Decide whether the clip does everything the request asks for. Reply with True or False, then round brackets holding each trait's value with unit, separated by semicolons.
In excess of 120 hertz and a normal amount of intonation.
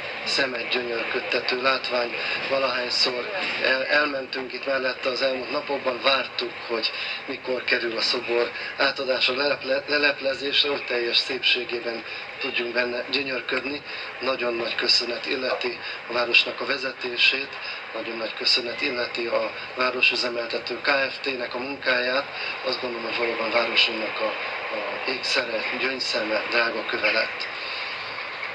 False (130 Hz; 2.0 semitones)